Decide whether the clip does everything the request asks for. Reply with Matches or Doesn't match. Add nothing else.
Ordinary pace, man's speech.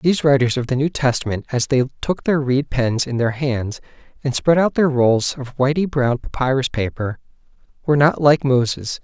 Matches